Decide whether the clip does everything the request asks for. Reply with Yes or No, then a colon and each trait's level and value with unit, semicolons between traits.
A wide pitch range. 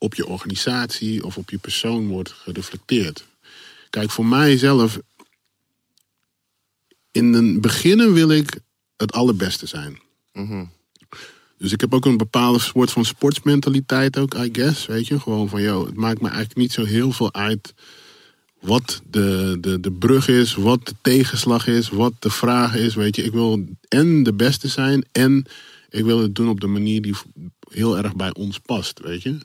No: average, 3.6 semitones